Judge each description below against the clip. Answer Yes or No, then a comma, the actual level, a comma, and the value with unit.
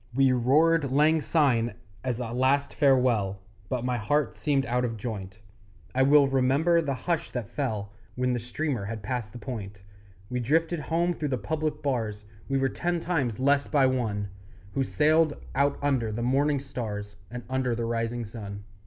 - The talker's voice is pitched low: Yes, low, 130 Hz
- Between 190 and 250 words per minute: No, average, 175 wpm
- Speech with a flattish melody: No, average, 3.8 semitones